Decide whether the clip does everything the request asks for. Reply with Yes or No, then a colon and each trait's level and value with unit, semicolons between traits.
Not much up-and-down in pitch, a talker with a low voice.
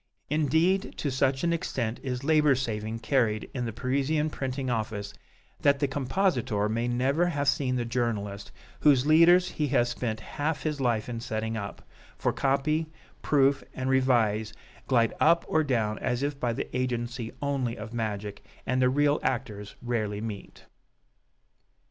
No: average, 4.0 semitones; low, 130 Hz